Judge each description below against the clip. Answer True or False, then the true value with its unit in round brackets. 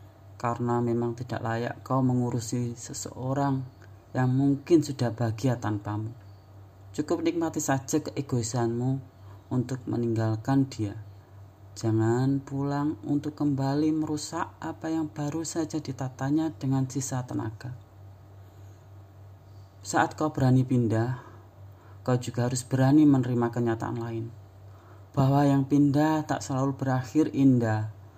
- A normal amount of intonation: True (4.6 semitones)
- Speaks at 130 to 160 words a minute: False (105 wpm)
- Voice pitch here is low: True (125 Hz)